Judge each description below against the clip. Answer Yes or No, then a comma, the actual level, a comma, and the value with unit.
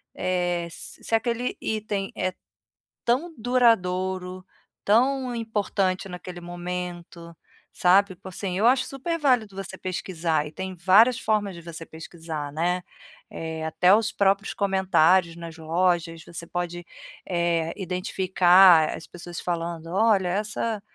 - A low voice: No, medium, 185 Hz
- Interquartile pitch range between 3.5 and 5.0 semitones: No, average, 3.1 semitones